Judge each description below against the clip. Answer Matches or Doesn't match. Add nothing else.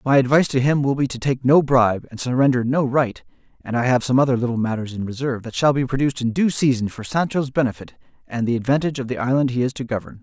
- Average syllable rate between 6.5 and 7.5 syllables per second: Matches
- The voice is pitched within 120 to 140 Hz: Matches